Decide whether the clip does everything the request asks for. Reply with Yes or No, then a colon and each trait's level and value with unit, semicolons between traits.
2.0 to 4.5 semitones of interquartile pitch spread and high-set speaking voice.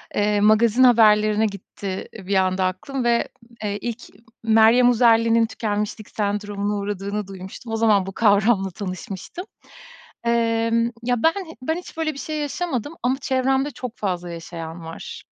Yes: average, 3.2 semitones; high, 215 Hz